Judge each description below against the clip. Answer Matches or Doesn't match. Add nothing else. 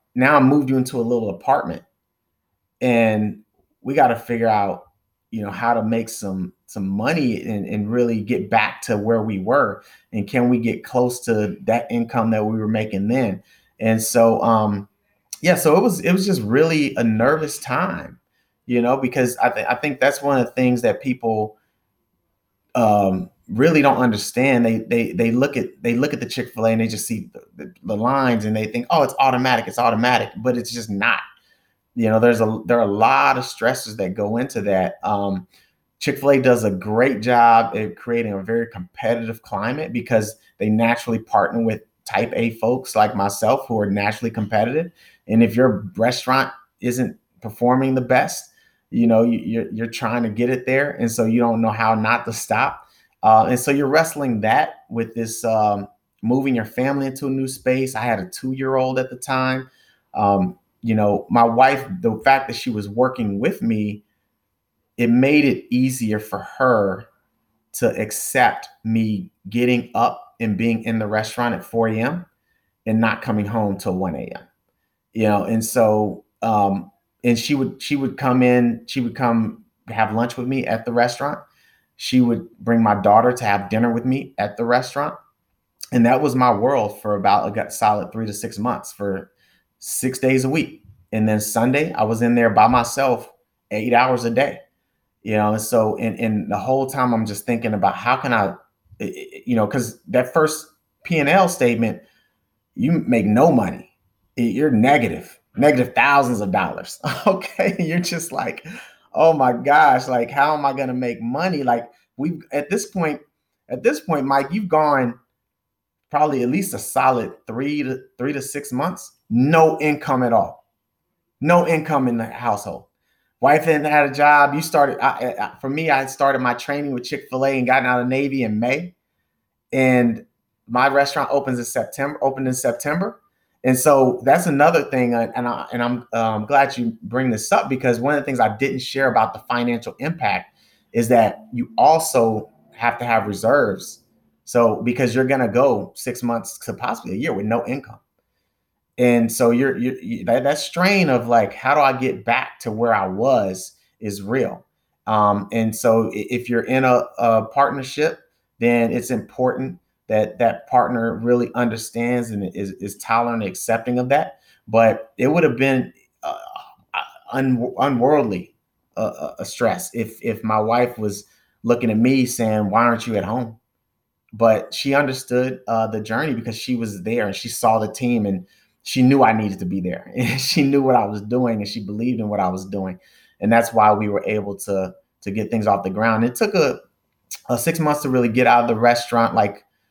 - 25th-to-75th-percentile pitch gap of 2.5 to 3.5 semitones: Matches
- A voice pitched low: Matches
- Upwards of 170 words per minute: Matches